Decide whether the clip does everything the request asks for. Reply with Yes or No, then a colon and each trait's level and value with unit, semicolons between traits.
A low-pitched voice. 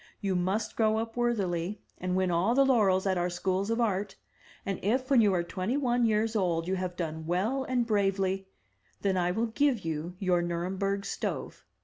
No: high, 195 Hz